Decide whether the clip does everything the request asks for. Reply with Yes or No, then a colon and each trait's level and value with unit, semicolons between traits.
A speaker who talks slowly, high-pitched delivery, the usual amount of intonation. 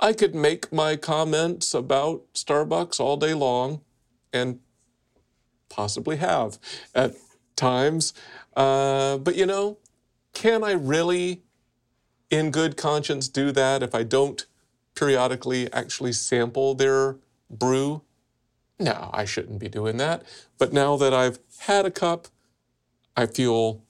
No: slow, 125 wpm; low, 135 Hz; average, 3.7 semitones